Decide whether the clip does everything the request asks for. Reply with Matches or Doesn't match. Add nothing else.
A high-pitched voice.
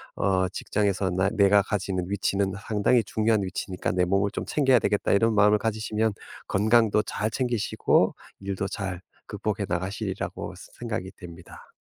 Doesn't match